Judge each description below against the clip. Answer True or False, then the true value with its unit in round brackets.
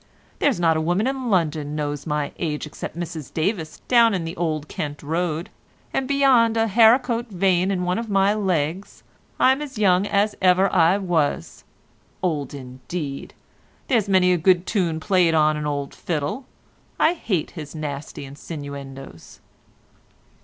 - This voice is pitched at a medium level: True (175 Hz)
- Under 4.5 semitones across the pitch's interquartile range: False (5.1 semitones)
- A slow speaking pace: False (155 wpm)